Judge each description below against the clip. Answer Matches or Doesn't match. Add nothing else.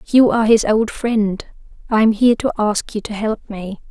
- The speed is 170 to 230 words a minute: Matches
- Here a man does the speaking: Doesn't match